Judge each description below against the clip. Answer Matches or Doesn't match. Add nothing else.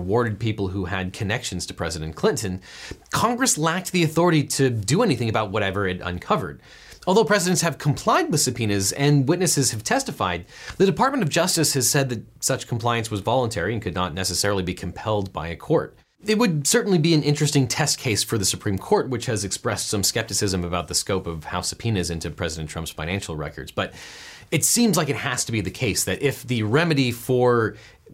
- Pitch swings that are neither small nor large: Doesn't match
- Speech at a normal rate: Matches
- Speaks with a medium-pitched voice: Doesn't match